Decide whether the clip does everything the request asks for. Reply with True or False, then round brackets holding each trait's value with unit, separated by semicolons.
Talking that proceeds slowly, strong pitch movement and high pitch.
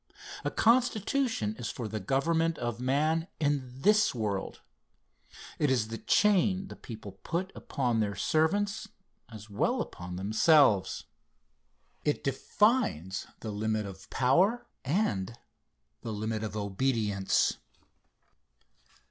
False (115 wpm; 8.0 semitones; 125 Hz)